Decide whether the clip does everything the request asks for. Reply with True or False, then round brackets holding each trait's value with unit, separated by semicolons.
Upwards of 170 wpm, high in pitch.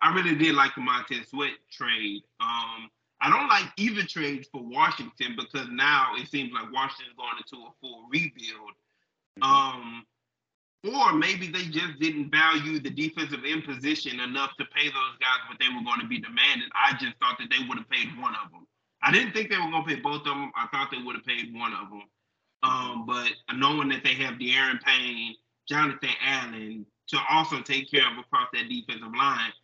False (200 wpm; 140 Hz)